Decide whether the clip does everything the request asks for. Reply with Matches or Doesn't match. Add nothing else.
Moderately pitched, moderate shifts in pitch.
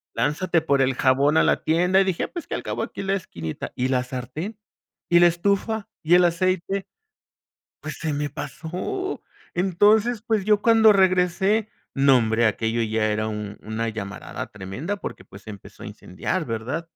Doesn't match